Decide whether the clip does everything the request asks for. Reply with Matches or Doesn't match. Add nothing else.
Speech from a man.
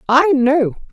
Doesn't match